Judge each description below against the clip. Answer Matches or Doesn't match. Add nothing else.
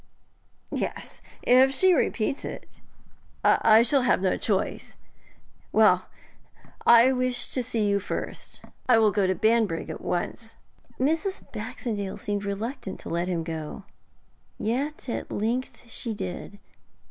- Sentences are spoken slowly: Matches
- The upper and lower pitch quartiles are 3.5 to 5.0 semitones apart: Matches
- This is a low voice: Doesn't match